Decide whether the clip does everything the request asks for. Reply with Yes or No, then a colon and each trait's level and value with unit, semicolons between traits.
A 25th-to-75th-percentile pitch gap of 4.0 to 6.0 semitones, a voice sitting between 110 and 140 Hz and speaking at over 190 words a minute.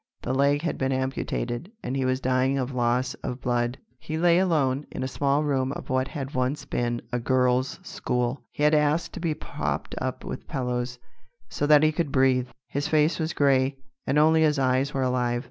No: average, 2.8 semitones; low, 135 Hz; average, 200 wpm